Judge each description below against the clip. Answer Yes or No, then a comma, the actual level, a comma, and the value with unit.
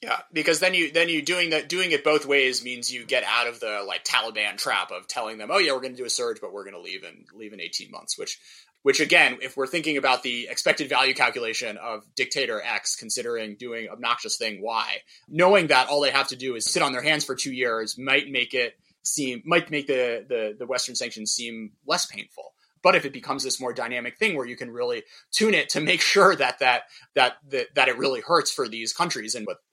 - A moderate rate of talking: No, fast, 235 wpm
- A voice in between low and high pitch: Yes, medium, 150 Hz